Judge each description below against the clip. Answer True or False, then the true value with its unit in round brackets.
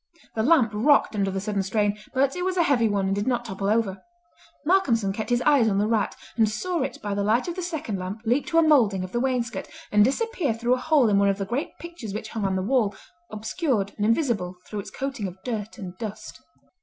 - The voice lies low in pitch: False (225 Hz)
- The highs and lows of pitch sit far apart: False (5.0 semitones)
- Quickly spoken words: True (245 wpm)